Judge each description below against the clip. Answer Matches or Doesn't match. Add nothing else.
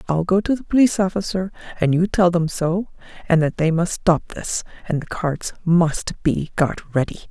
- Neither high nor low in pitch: Matches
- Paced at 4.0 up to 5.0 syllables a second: Matches